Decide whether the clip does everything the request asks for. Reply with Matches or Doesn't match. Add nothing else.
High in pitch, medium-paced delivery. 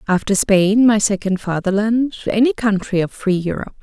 Matches